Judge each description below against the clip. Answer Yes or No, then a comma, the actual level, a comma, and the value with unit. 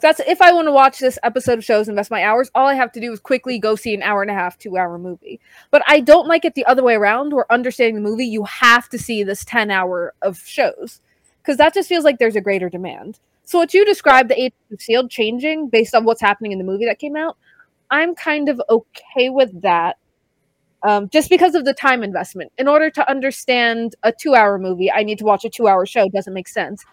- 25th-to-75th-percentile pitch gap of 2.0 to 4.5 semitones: No, average, 5.2 semitones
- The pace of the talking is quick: Yes, fast, 245 wpm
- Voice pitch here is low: No, high, 235 Hz